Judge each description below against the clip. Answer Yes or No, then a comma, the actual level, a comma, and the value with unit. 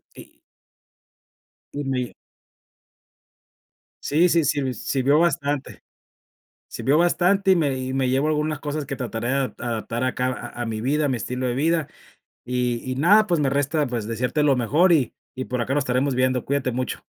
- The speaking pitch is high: No, low, 135 Hz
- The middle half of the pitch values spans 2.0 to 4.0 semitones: Yes, average, 3.0 semitones